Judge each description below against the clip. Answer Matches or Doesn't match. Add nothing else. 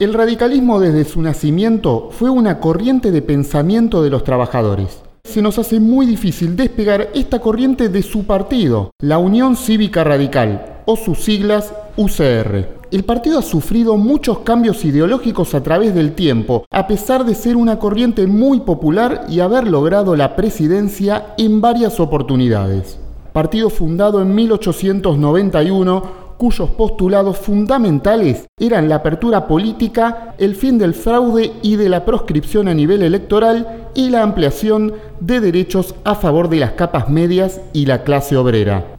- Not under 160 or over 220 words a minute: Doesn't match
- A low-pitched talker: Doesn't match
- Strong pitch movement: Matches